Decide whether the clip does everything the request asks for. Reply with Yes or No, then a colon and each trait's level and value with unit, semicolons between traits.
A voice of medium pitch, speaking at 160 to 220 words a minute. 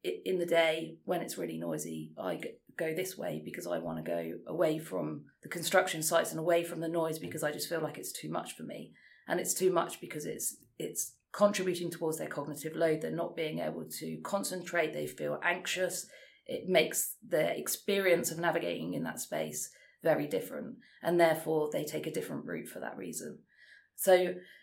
Yes: medium, 165 Hz; average, 190 wpm